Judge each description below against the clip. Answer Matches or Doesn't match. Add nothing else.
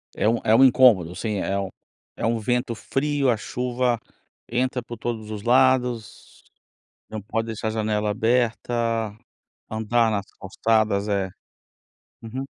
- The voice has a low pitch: Matches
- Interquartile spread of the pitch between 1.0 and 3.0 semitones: Matches